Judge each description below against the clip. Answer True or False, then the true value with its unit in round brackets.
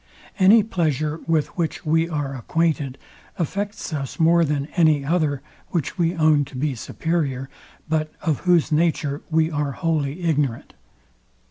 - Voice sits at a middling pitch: True (155 Hz)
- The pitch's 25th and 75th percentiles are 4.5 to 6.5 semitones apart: False (2.7 semitones)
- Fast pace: False (140 wpm)